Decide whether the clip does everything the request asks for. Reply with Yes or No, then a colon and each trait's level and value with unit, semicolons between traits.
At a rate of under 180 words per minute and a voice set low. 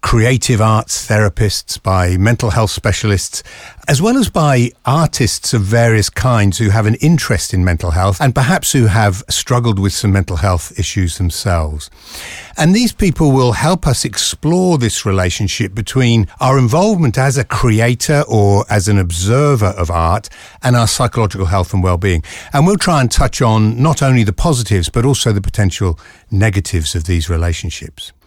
Yes: average, 165 wpm; low, 110 Hz